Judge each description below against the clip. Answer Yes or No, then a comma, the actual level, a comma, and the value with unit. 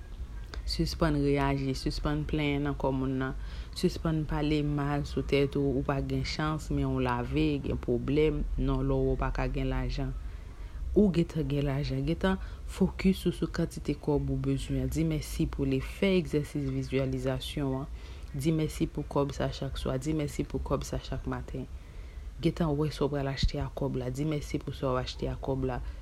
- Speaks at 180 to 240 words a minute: Yes, average, 185 wpm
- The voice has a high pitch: No, medium, 140 Hz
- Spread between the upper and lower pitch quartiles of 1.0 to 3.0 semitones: Yes, narrow, 2.5 semitones